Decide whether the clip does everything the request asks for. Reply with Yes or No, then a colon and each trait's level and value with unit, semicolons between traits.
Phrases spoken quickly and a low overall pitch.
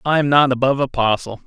Yes: fast, 245 wpm; low, 130 Hz